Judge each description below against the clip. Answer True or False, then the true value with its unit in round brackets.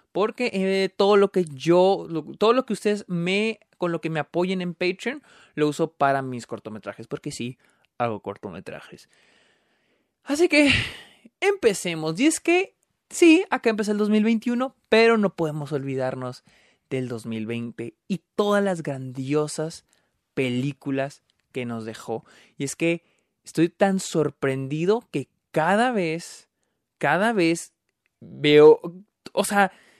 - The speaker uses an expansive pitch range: True (6.8 semitones)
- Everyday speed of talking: True (135 wpm)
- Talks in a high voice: False (170 Hz)